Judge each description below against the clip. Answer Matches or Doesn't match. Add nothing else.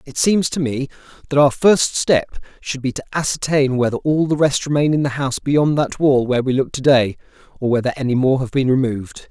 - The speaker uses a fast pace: Matches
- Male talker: Matches